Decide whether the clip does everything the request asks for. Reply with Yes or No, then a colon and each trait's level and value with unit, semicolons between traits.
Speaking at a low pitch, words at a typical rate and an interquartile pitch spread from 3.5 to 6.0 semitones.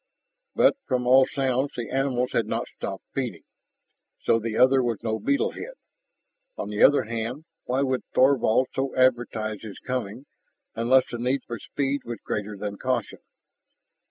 No: low, 125 Hz; average, 155 wpm; average, 2.8 semitones